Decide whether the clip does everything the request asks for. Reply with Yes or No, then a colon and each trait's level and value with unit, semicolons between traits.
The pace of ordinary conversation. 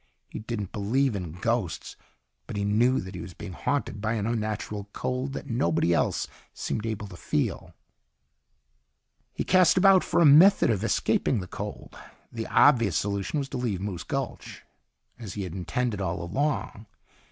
Yes: average, 165 wpm